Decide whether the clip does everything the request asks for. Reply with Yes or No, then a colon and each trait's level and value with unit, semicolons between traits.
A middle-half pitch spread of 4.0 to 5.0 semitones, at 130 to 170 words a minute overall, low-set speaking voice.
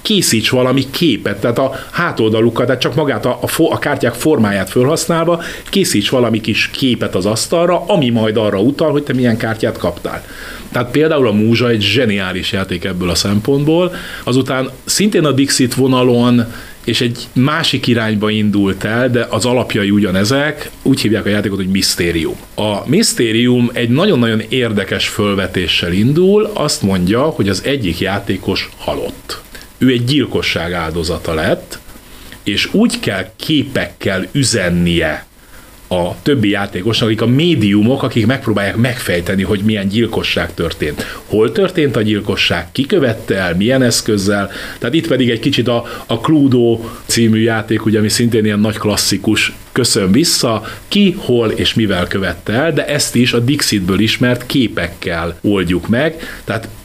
Yes: average, 4.5 semitones; average, 150 wpm; low, 115 Hz